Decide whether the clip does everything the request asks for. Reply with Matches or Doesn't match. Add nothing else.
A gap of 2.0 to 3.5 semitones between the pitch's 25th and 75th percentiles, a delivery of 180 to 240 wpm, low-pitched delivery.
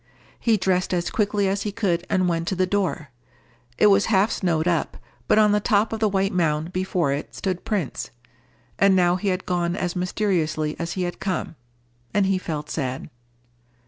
Doesn't match